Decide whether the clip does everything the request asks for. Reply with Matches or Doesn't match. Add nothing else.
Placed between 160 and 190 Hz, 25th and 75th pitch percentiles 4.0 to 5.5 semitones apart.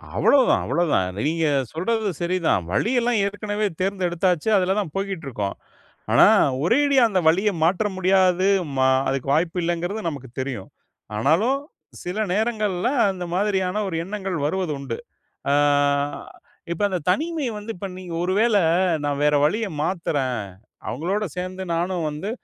Matches